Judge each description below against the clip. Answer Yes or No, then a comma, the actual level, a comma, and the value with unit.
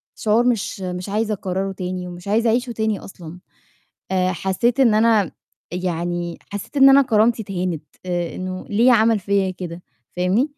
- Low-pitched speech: No, high, 195 Hz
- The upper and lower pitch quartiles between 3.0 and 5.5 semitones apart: Yes, average, 3.8 semitones